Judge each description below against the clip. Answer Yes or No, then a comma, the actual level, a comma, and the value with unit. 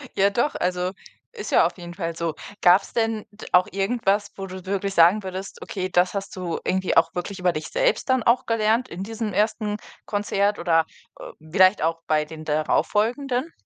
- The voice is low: No, high, 195 Hz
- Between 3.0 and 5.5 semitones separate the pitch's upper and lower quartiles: Yes, average, 3.3 semitones